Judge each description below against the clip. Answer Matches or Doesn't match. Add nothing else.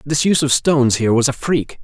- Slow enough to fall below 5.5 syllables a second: Doesn't match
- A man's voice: Matches